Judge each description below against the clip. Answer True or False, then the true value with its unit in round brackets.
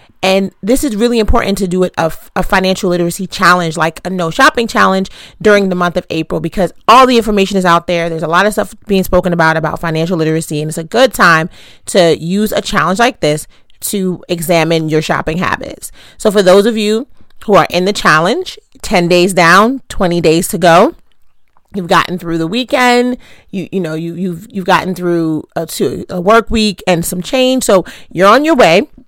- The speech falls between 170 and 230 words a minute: True (205 wpm)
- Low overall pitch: False (185 Hz)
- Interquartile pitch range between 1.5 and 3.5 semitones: False (3.9 semitones)